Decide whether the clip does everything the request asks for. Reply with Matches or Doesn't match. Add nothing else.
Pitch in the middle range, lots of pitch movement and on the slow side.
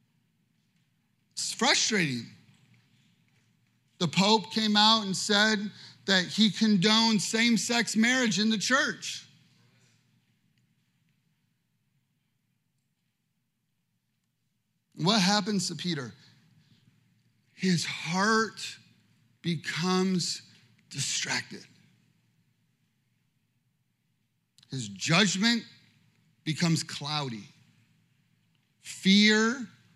Matches